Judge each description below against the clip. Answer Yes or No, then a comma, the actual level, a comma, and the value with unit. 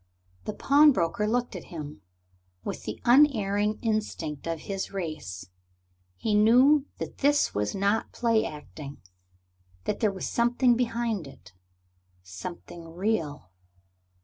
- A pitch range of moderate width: No, wide, 6.8 semitones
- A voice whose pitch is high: Yes, high, 205 Hz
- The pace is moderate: No, slow, 120 wpm